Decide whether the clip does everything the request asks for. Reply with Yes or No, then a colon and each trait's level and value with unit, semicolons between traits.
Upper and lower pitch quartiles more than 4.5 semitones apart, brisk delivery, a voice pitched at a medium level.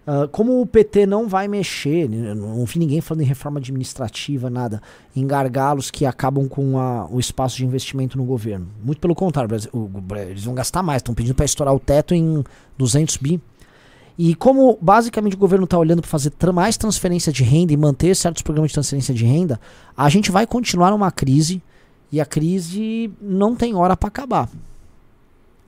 Yes: wide, 5.6 semitones; fast, 190 wpm; medium, 150 Hz